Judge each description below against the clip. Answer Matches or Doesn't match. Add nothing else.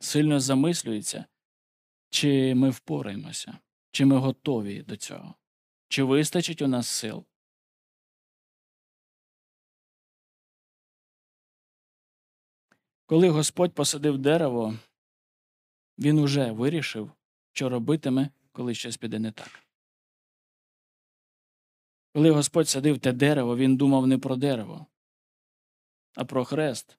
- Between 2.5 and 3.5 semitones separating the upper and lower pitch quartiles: Matches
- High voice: Doesn't match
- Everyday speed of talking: Doesn't match